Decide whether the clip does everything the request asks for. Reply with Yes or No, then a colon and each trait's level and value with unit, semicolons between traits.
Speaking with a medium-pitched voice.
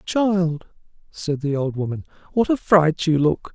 Yes: medium, 165 Hz